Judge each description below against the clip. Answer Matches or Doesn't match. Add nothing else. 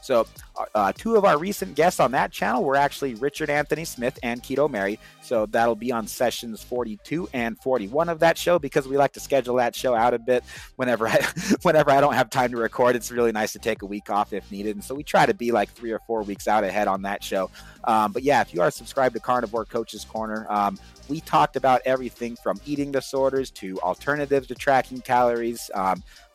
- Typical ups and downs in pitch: Matches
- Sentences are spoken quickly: Matches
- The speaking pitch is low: Matches